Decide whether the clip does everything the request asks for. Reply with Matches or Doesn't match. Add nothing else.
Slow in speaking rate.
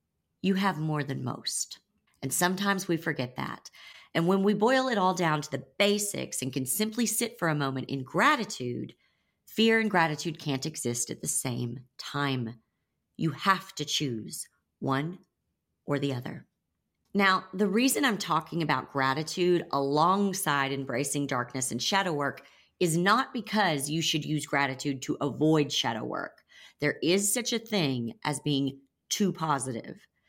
Doesn't match